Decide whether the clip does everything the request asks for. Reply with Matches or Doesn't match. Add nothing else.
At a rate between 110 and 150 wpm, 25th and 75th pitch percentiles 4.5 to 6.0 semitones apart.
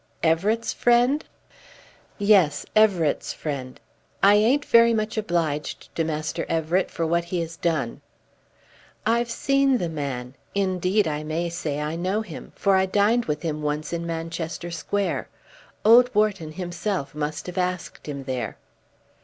Matches